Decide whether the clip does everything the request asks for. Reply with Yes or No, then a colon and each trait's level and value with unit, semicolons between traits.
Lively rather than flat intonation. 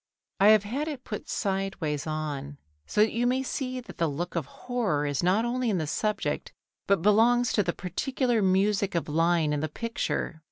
Yes: wide, 6.5 semitones